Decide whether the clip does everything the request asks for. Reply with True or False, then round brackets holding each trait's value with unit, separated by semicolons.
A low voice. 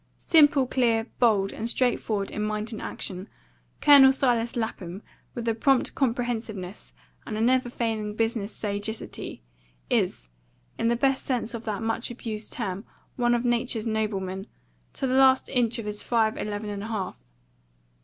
False (225 Hz)